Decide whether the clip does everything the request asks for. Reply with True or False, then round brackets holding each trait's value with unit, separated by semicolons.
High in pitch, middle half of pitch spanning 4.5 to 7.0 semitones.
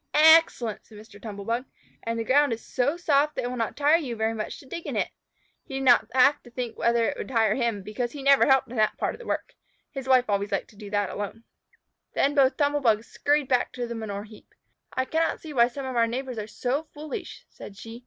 False (245 Hz; 3.8 semitones)